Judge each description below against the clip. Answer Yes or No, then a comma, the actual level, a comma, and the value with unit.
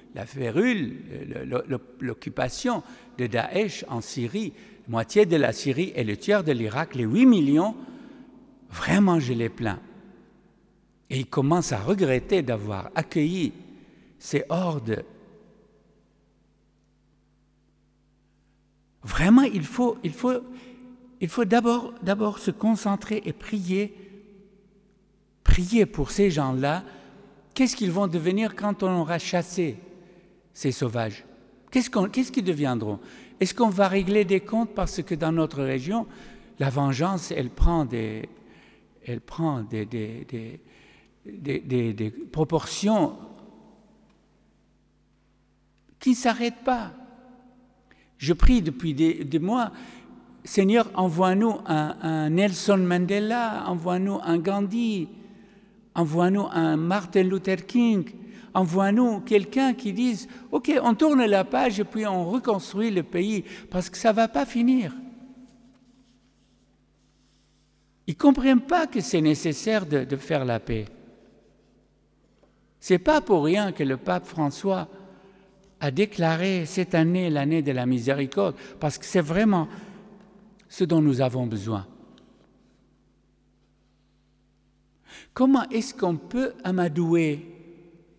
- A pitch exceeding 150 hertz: Yes, medium, 185 Hz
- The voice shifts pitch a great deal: Yes, wide, 6.2 semitones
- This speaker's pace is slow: Yes, slow, 120 wpm